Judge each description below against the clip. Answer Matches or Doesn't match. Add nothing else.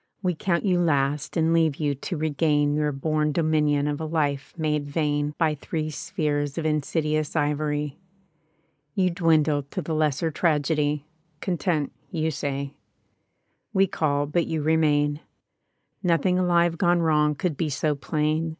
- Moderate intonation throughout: Doesn't match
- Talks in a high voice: Doesn't match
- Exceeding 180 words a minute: Doesn't match